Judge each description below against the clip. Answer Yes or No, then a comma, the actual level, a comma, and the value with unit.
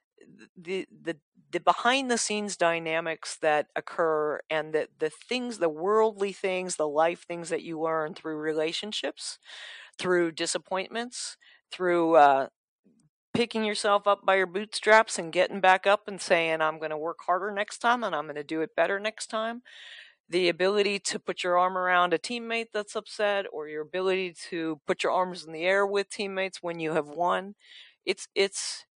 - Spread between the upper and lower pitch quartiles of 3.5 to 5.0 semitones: Yes, average, 4.0 semitones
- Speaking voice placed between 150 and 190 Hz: Yes, medium, 185 Hz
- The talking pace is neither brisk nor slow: Yes, average, 175 wpm